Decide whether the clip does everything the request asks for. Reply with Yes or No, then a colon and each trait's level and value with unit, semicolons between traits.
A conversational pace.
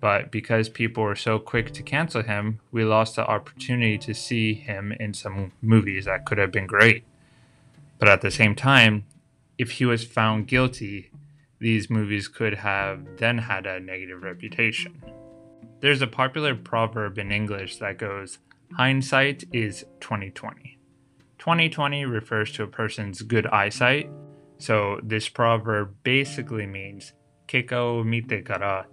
Yes: average, 145 wpm